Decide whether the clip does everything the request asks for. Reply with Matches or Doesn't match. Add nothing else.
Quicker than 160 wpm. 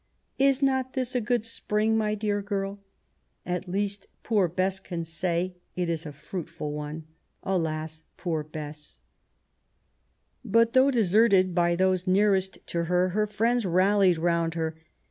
Doesn't match